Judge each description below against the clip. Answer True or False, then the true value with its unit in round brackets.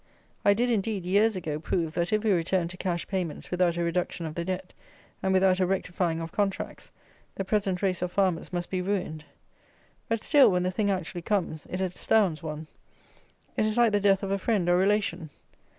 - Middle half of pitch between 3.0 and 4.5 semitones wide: False (2.6 semitones)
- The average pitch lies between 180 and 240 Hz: True (185 Hz)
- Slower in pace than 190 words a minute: False (200 wpm)